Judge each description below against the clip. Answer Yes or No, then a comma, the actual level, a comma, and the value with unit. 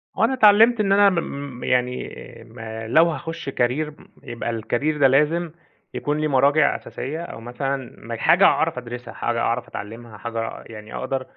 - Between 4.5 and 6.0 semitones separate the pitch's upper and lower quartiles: Yes, average, 5.1 semitones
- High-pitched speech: No, low, 135 Hz